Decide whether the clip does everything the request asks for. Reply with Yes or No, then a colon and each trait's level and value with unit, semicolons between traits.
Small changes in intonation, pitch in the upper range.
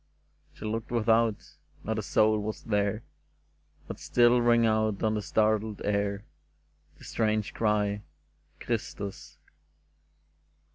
No: narrow, 1.5 semitones; low, 110 Hz